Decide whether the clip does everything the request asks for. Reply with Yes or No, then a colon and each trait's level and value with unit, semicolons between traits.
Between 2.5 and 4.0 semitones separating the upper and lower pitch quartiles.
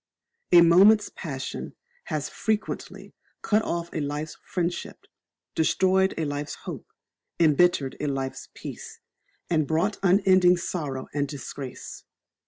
No: average, 4.5 semitones